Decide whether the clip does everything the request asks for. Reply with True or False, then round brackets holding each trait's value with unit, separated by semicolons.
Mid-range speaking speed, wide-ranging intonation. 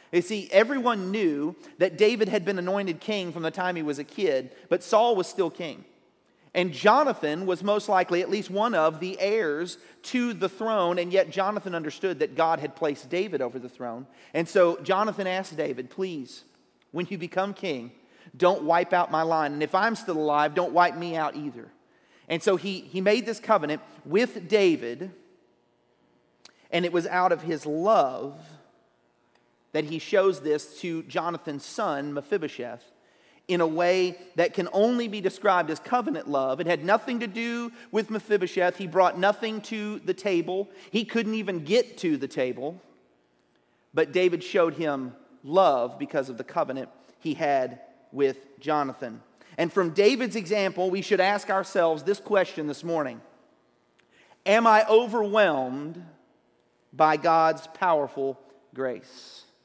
False (160 wpm; 4.6 semitones)